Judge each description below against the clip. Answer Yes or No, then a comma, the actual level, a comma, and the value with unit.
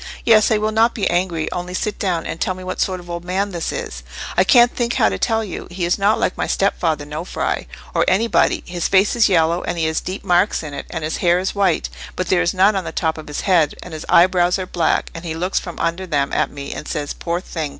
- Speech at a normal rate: No, fast, 260 wpm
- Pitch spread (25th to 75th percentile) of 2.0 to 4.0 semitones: Yes, average, 2.9 semitones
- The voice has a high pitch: No, medium, 180 Hz